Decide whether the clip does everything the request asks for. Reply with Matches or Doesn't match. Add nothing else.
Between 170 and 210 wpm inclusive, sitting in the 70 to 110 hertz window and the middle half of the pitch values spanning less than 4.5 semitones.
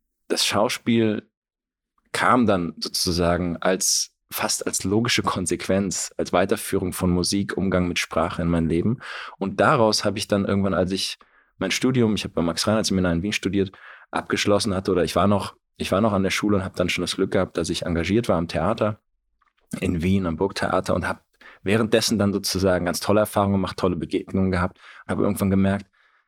Matches